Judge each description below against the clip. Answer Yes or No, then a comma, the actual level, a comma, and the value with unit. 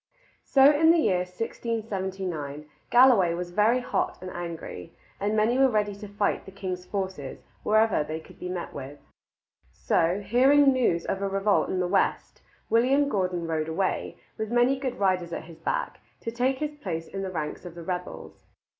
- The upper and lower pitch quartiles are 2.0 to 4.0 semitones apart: No, average, 5.3 semitones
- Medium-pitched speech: No, high, 195 Hz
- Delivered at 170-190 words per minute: Yes, average, 180 wpm